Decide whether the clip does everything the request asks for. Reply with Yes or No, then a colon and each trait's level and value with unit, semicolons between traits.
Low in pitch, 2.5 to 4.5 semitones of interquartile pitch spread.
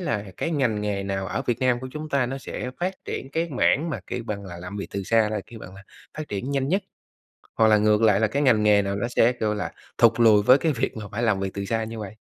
Yes: low, 110 Hz; average, 4.1 semitones